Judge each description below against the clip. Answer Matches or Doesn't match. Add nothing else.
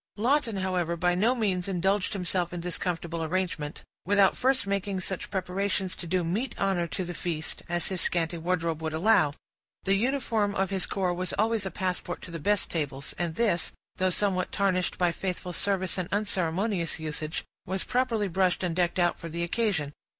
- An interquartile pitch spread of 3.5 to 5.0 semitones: Doesn't match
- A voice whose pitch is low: Doesn't match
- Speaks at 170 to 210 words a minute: Matches